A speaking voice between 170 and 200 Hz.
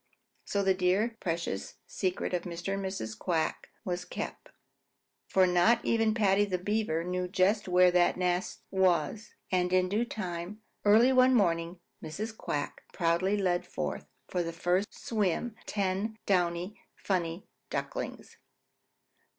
Yes: medium, 185 Hz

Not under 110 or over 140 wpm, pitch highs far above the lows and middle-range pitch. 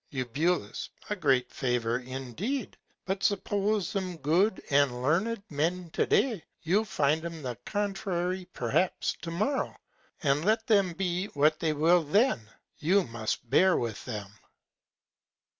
Yes: slow, 135 wpm; wide, 6.1 semitones; medium, 170 Hz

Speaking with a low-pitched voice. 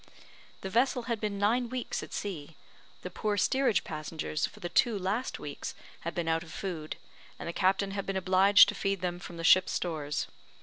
No: high, 190 Hz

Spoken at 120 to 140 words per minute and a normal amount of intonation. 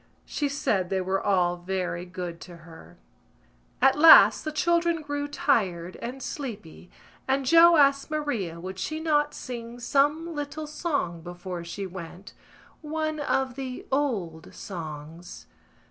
No: slow, 135 wpm; wide, 8.7 semitones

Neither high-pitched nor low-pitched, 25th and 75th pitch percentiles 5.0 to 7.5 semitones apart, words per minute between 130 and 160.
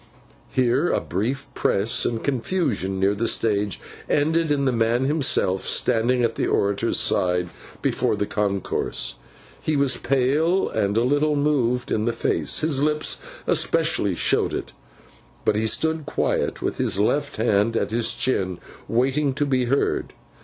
No: low, 125 Hz; wide, 5.4 semitones; average, 150 wpm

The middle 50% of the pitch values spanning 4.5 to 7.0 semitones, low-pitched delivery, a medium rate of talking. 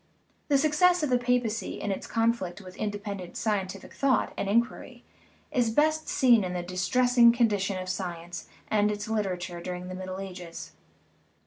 No: average, 4.8 semitones; high, 205 Hz; average, 170 wpm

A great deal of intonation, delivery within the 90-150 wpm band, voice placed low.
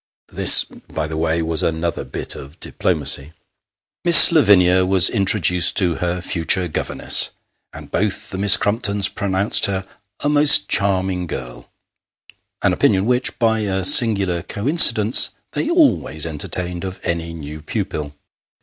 No: average, 3.7 semitones; average, 140 wpm; very low, 95 Hz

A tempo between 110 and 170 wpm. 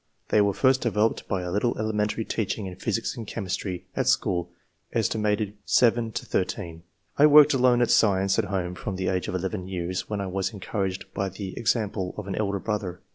No: average, 190 wpm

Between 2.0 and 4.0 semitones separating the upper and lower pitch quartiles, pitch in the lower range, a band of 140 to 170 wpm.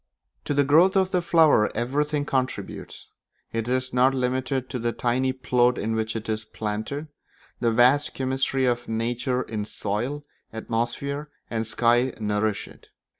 Yes: average, 3.2 semitones; low, 125 Hz; average, 150 wpm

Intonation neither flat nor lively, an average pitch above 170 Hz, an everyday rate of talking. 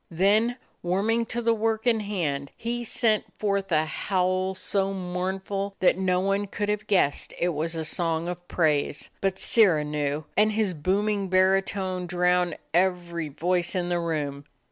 Yes: average, 3.0 semitones; medium, 185 Hz; average, 160 wpm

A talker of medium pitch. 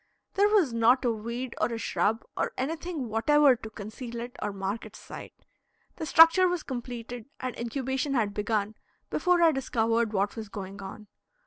No: high, 235 Hz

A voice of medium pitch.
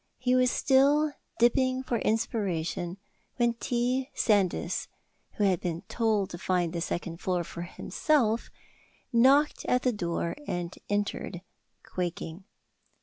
No: high, 210 Hz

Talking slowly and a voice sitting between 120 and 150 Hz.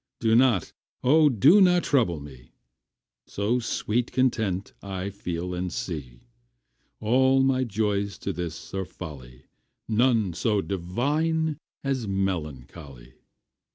No: slow, 115 wpm; low, 100 Hz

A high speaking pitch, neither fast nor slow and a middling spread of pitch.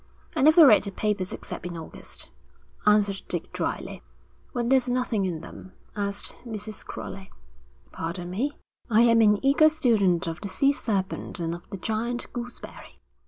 Yes: high, 210 Hz; average, 160 wpm; average, 4.4 semitones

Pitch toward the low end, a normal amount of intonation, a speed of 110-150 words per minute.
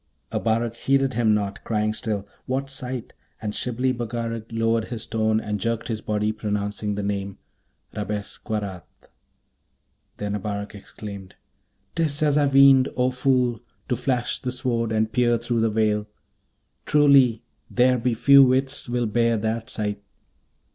Yes: low, 115 Hz; average, 3.2 semitones; average, 140 wpm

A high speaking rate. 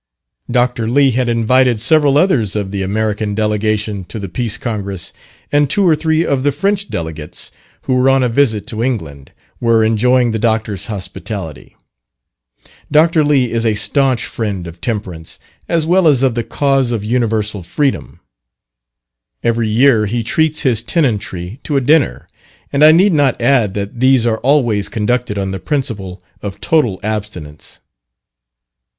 No: average, 155 wpm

